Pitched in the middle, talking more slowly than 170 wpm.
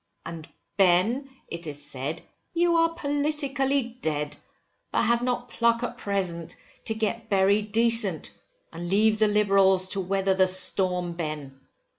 No: high, 200 Hz; average, 140 wpm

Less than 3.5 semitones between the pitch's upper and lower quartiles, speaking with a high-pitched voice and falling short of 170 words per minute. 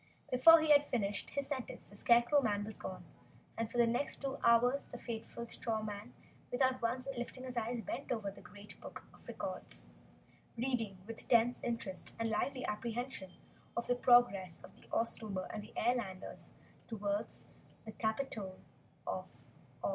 Yes: average, 2.9 semitones; high, 230 Hz; average, 160 wpm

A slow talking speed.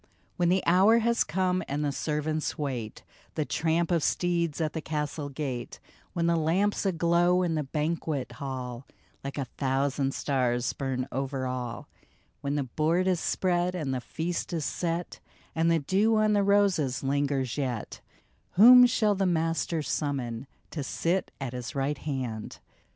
No: average, 160 wpm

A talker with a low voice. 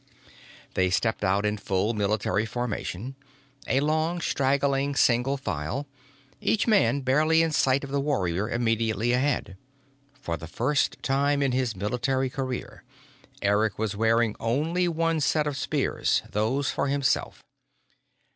Yes: low, 130 Hz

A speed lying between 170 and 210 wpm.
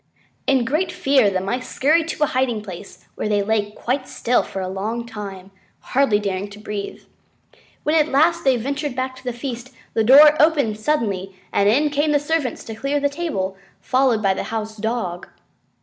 Yes: average, 190 wpm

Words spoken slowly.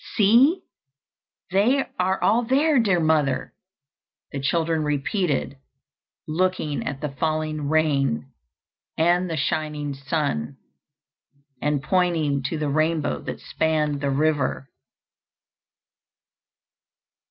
Yes: slow, 95 wpm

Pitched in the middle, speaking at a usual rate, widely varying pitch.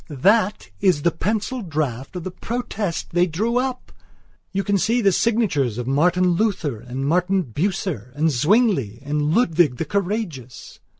Yes: medium, 175 Hz; average, 155 wpm; wide, 6.1 semitones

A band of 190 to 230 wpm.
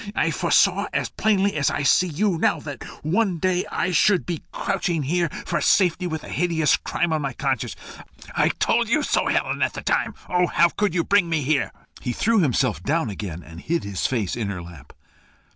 Yes: fast, 205 wpm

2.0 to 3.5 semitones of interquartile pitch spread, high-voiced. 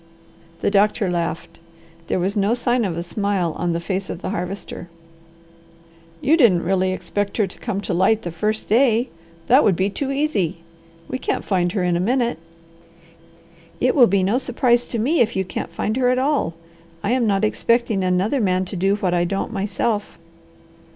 No: average, 4.5 semitones; high, 200 Hz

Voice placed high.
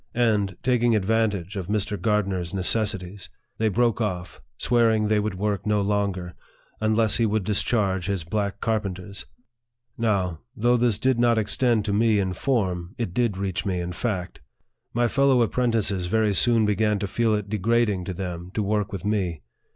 No: low, 105 Hz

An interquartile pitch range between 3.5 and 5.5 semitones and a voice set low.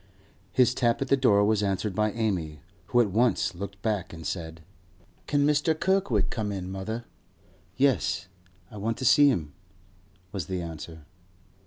Yes: average, 5.1 semitones; low, 105 Hz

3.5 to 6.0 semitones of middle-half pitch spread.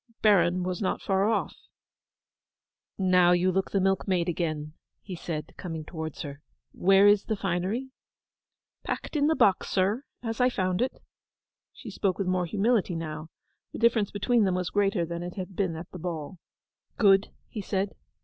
No: average, 2.8 semitones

